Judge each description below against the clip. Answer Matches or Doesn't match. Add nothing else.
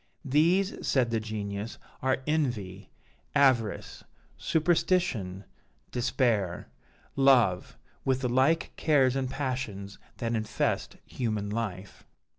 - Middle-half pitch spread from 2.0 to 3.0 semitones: Doesn't match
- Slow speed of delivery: Matches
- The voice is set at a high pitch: Doesn't match